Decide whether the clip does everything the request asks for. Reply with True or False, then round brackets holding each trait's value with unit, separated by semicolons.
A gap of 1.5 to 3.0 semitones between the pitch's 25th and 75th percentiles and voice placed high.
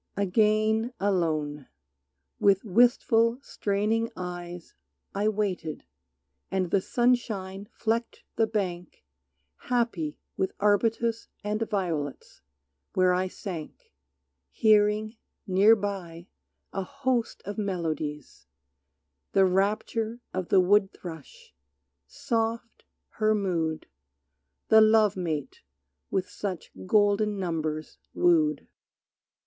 False (3.7 semitones; 200 Hz)